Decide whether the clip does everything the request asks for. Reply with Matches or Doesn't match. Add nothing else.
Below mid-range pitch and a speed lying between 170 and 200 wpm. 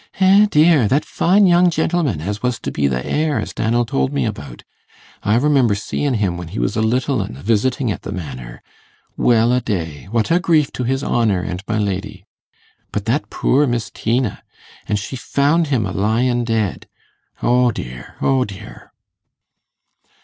Matches